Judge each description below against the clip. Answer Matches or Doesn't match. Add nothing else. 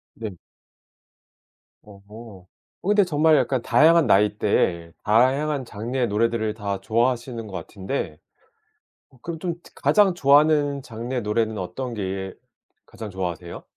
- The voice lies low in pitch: Matches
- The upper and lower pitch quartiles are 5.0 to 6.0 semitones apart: Matches